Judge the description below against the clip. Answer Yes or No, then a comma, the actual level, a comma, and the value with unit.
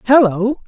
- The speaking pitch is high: Yes, high, 230 Hz